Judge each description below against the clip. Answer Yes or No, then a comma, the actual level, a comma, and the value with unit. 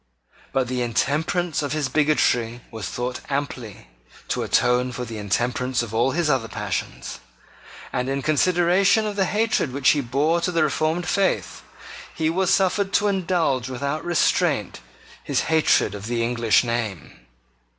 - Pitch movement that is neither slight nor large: No, wide, 5.9 semitones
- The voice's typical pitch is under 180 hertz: Yes, medium, 140 Hz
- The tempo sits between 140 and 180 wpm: Yes, average, 150 wpm